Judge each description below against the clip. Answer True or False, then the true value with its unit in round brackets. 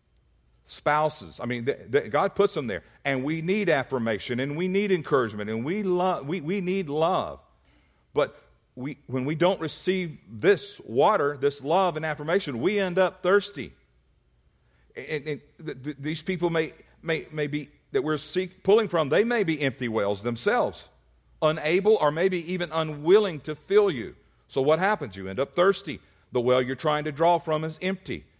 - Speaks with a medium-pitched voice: True (155 Hz)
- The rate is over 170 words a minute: True (180 wpm)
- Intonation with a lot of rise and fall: True (6.6 semitones)